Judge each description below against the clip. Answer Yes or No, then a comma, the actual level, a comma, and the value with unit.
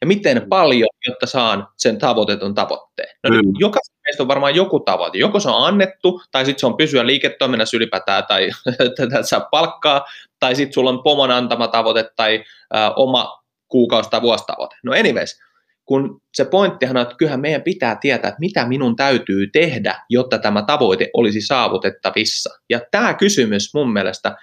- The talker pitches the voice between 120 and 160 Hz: Yes, low, 130 Hz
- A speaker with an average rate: No, fast, 170 wpm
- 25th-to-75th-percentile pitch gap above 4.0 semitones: Yes, average, 4.6 semitones